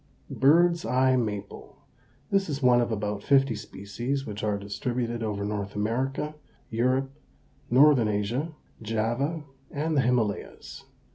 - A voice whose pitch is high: No, low, 120 Hz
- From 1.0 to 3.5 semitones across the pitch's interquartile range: No, average, 4.5 semitones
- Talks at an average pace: No, slow, 125 wpm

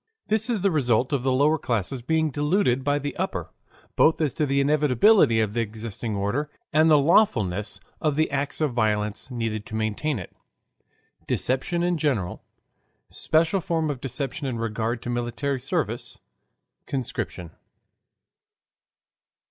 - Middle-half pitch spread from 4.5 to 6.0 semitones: Yes, average, 5.1 semitones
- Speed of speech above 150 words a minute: No, average, 145 wpm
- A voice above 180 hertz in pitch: No, low, 135 Hz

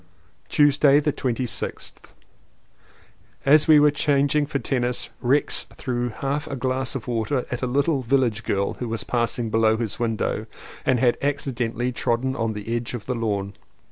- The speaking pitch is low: Yes, low, 125 Hz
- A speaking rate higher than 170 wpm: No, average, 160 wpm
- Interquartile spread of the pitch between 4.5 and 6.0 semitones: No, average, 3.2 semitones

